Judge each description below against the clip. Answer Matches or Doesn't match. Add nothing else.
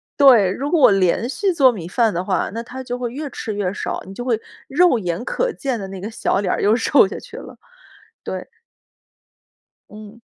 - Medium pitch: Doesn't match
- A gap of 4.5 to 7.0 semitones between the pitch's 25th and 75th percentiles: Matches